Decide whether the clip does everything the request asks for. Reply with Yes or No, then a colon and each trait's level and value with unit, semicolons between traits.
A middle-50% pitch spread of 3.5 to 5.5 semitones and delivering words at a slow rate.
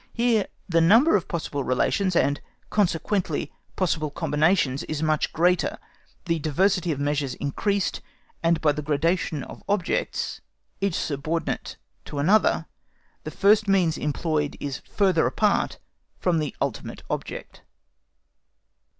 Yes: average, 4.6 semitones; slow, 125 wpm